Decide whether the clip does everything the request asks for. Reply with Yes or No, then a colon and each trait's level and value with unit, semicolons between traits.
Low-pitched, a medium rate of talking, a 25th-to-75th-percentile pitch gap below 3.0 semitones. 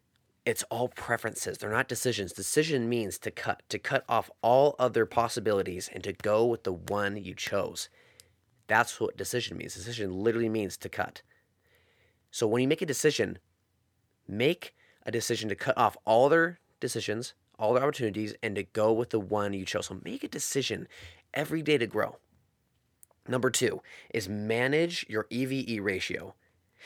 No: low, 115 Hz; average, 165 wpm; average, 3.3 semitones